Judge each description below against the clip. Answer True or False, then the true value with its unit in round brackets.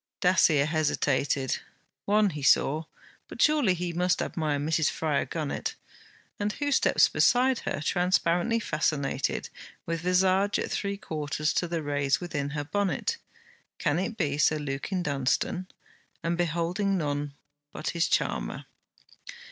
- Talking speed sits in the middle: False (130 wpm)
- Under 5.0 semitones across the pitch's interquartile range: True (4.2 semitones)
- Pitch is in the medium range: True (165 Hz)